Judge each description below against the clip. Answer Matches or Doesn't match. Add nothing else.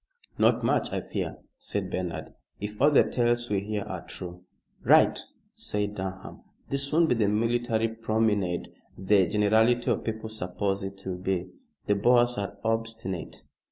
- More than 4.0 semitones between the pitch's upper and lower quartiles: Doesn't match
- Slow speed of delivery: Doesn't match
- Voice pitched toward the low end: Matches